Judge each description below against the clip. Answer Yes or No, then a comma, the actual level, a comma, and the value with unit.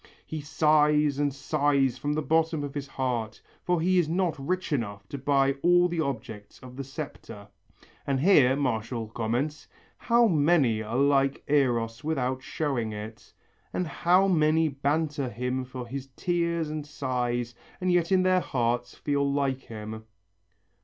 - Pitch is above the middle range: No, medium, 140 Hz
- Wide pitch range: No, average, 4.1 semitones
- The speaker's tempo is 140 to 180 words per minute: Yes, average, 155 wpm